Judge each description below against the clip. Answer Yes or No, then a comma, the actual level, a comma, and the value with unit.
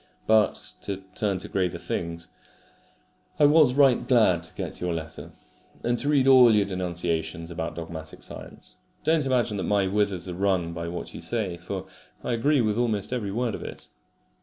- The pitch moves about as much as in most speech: No, wide, 5.7 semitones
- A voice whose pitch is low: Yes, low, 100 Hz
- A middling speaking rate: Yes, average, 180 wpm